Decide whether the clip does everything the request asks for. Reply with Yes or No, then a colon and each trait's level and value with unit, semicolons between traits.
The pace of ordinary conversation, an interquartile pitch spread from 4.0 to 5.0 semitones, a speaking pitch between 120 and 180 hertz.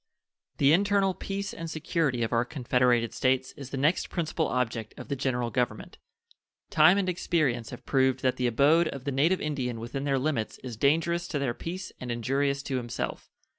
Yes: average, 185 wpm; average, 4.7 semitones; low, 135 Hz